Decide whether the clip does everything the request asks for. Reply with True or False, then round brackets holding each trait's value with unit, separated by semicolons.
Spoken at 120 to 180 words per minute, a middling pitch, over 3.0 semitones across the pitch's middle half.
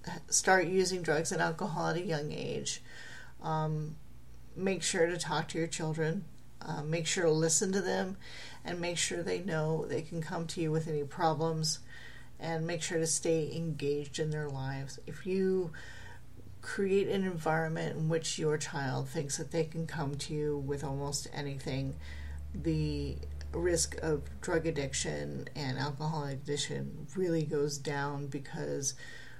False (155 wpm; 155 Hz; 2.7 semitones)